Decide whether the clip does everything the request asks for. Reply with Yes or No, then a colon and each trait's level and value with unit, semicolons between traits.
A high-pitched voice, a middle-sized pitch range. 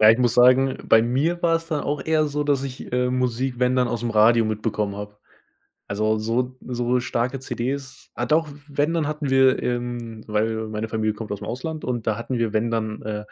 No: low, 120 Hz; average, 3.3 semitones